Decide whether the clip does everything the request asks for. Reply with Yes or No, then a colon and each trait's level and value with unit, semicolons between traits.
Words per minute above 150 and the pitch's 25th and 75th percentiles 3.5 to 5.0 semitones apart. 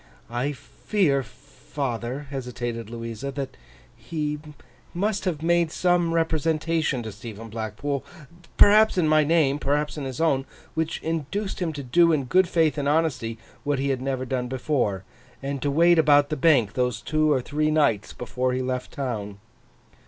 Yes: average, 160 wpm; average, 4.3 semitones